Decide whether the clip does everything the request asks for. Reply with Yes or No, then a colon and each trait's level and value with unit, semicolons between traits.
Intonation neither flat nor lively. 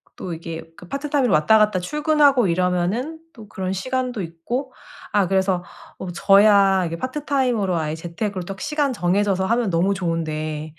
No: wide, 6.1 semitones